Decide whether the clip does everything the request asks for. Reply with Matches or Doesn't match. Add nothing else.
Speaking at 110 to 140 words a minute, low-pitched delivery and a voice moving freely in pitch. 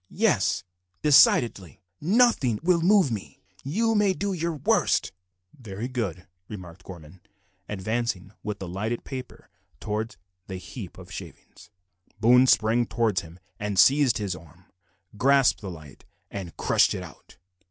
Matches